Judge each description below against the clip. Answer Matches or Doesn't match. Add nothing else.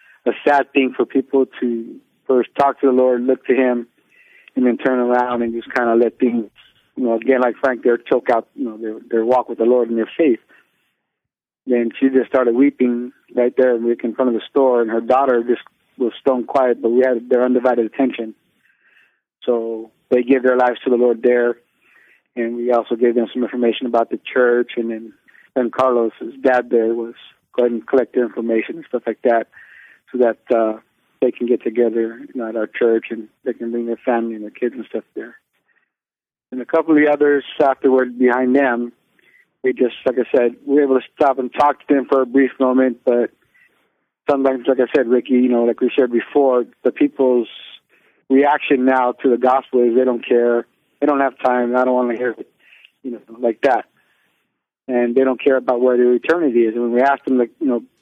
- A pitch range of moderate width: Doesn't match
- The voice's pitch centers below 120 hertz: Doesn't match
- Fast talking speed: Matches